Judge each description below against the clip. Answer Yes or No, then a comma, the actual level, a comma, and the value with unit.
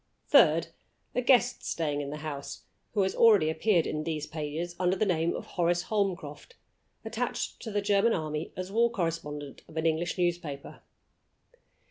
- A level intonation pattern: No, average, 4.5 semitones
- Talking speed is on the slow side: No, average, 160 wpm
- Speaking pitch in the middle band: Yes, medium, 170 Hz